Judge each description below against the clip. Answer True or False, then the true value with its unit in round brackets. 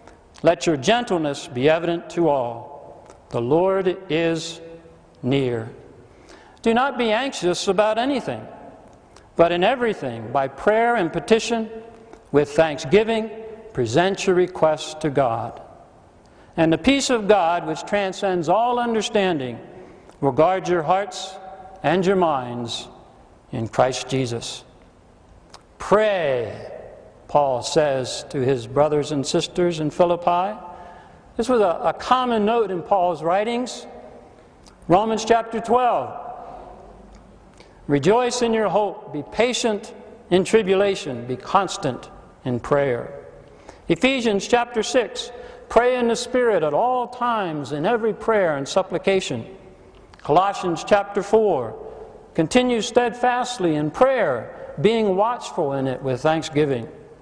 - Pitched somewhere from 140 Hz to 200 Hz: True (185 Hz)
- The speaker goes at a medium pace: False (115 wpm)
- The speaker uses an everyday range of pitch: False (7.1 semitones)